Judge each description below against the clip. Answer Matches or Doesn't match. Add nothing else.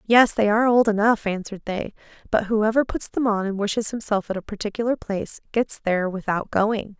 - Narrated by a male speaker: Doesn't match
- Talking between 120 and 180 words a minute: Doesn't match